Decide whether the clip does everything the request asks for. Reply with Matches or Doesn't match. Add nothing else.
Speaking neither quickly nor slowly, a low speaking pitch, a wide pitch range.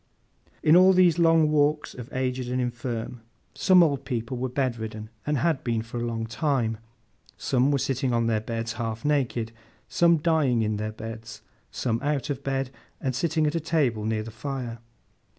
Doesn't match